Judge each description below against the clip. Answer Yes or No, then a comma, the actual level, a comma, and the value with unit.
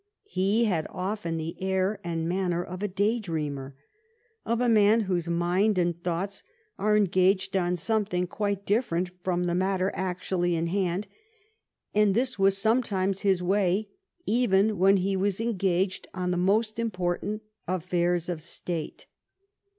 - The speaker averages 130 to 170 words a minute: Yes, average, 150 wpm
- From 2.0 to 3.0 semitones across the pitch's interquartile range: Yes, average, 2.7 semitones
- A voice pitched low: No, high, 190 Hz